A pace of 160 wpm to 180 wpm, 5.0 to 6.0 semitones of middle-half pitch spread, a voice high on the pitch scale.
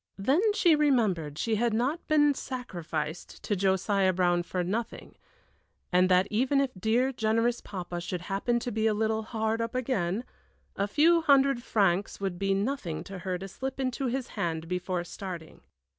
Yes: average, 170 wpm; wide, 5.6 semitones; high, 210 Hz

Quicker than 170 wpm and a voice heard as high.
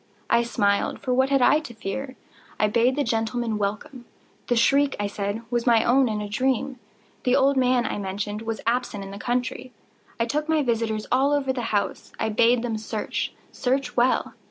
Yes: average, 185 wpm; high, 240 Hz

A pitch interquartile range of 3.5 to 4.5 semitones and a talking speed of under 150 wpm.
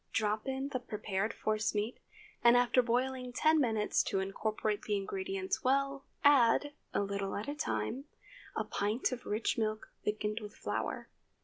No: average, 4.1 semitones; average, 155 wpm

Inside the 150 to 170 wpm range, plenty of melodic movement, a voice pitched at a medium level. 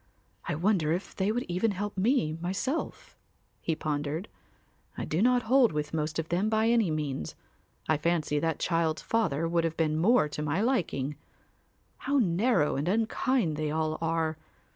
Yes: average, 165 wpm; wide, 5.9 semitones; medium, 165 Hz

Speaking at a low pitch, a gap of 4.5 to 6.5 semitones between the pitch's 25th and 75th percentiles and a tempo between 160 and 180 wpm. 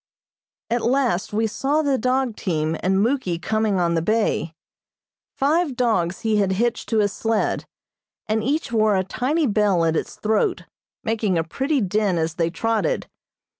No: high, 215 Hz; average, 5.1 semitones; average, 165 wpm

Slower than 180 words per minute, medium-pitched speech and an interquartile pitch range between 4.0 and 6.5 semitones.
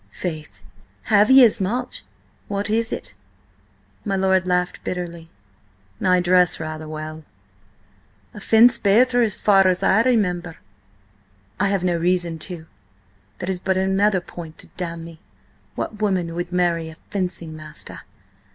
No: average, 140 wpm; medium, 180 Hz; average, 3.2 semitones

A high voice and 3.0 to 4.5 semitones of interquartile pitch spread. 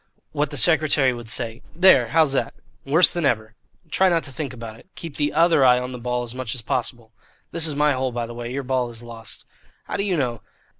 No: low, 130 Hz; average, 4.1 semitones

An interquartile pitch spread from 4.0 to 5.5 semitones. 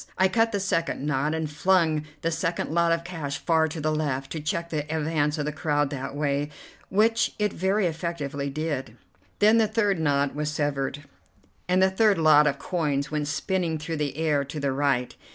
No: average, 2.9 semitones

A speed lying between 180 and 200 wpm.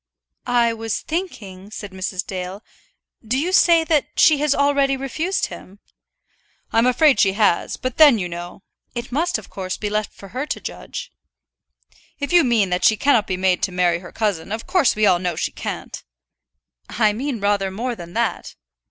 Yes: average, 190 wpm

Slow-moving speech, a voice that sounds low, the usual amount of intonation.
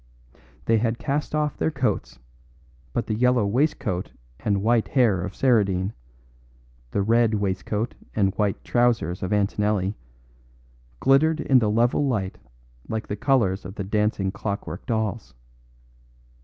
Yes: slow, 130 wpm; low, 105 Hz; average, 3.6 semitones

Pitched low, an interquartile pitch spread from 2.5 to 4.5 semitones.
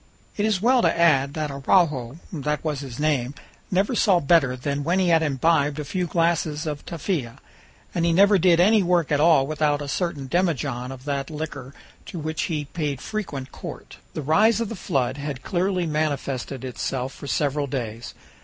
No: medium, 150 Hz; average, 3.9 semitones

